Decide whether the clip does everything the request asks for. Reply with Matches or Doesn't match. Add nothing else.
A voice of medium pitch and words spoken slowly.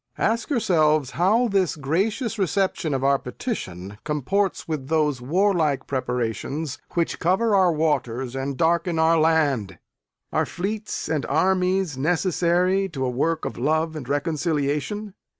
Matches